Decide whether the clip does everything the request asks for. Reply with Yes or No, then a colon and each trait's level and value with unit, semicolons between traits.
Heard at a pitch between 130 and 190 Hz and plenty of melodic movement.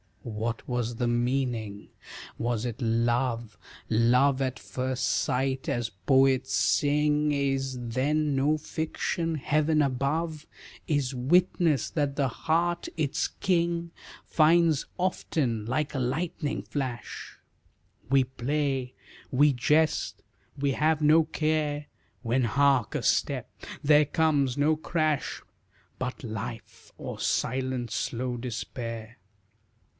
No: low, 135 Hz; average, 3.9 semitones